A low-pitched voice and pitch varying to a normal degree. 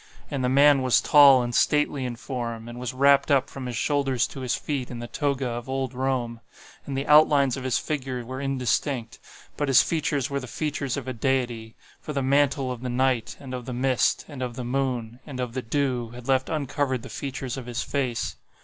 No: low, 130 Hz; narrow, 2.1 semitones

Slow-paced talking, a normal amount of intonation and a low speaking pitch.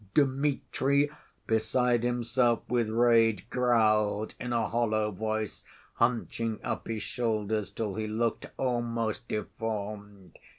No: slow, 110 wpm; narrow, 2.2 semitones; low, 115 Hz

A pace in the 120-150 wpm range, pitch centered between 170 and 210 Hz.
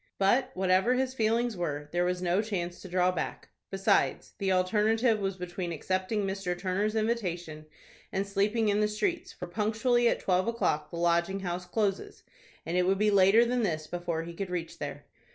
No: average, 185 wpm; high, 190 Hz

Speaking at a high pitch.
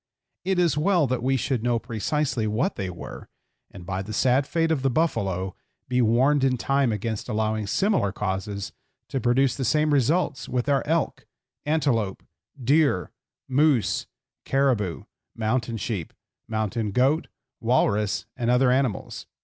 No: low, 125 Hz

